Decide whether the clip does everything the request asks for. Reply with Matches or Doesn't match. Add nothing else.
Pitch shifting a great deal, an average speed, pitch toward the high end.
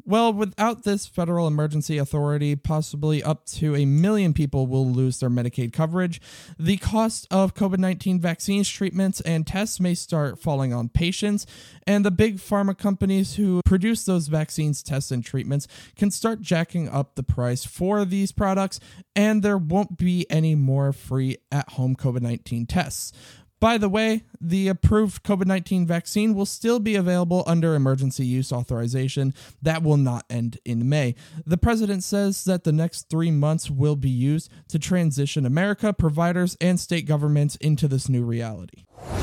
Doesn't match